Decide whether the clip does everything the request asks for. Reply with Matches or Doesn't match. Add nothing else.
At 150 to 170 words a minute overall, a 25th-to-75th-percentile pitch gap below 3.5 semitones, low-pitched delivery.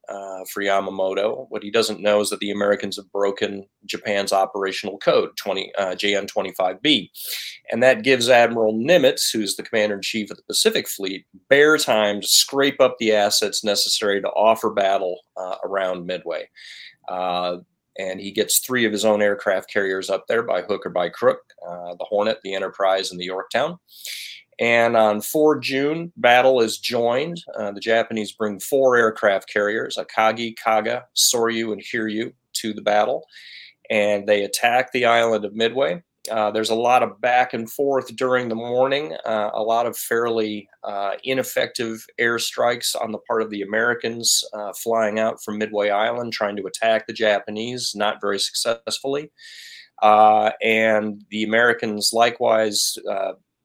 Matches